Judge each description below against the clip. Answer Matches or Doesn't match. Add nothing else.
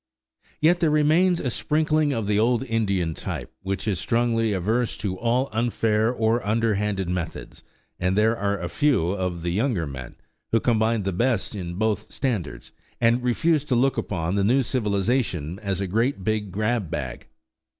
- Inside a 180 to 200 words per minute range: Doesn't match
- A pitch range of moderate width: Matches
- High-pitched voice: Doesn't match